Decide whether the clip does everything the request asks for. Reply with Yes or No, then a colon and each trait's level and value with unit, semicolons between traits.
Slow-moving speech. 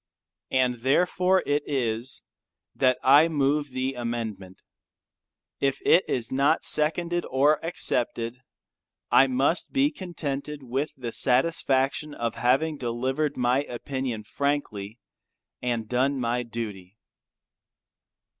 Yes: slow, 110 wpm